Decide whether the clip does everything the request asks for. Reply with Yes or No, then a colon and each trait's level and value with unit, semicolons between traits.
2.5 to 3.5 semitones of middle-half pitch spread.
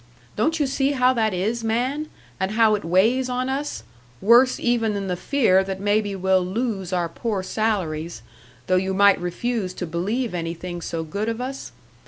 No: average, 4.8 semitones